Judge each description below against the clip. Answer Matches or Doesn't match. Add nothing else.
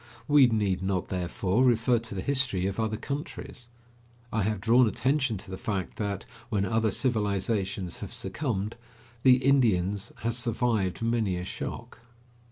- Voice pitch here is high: Doesn't match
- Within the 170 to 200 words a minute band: Doesn't match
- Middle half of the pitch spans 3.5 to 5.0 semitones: Matches